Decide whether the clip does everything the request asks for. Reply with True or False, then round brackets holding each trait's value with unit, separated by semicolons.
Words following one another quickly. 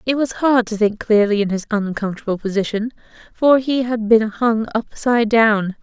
False (175 wpm)